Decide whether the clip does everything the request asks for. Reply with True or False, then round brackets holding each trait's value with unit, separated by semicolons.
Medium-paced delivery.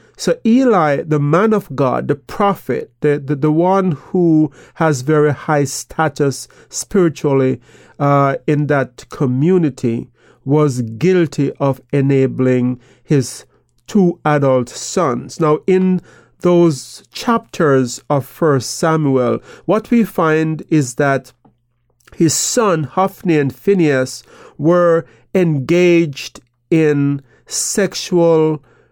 False (105 wpm)